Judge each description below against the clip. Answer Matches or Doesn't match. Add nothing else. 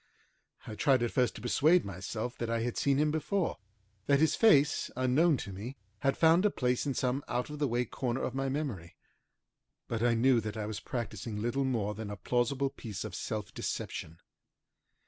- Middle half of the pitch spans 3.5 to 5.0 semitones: Matches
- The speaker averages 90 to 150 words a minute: Doesn't match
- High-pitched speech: Doesn't match